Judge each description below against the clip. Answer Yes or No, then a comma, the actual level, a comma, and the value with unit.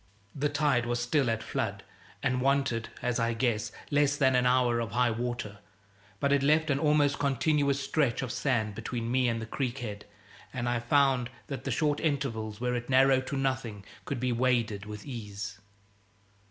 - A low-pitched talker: Yes, low, 125 Hz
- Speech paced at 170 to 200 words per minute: Yes, average, 180 wpm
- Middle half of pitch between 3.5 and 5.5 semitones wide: No, average, 3.1 semitones